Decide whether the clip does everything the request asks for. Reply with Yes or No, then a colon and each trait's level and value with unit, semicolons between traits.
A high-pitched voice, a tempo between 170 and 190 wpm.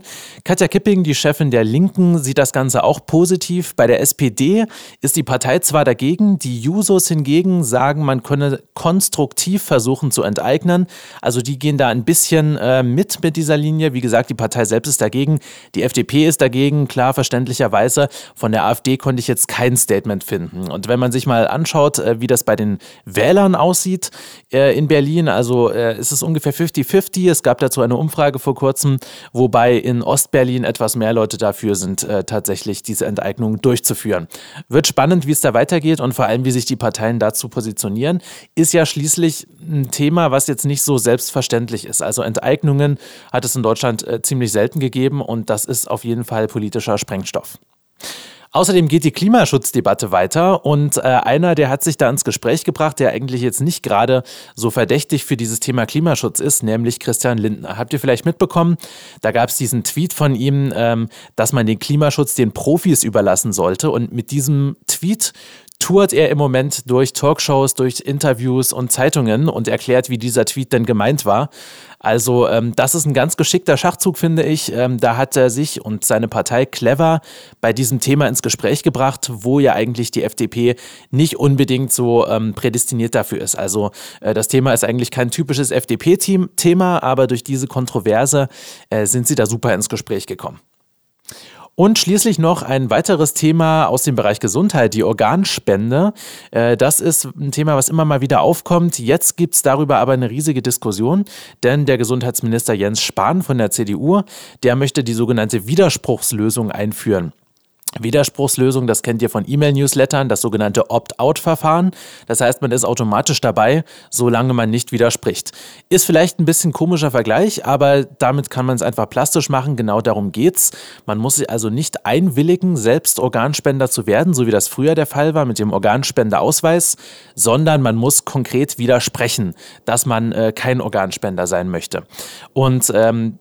No: low, 135 Hz; average, 175 wpm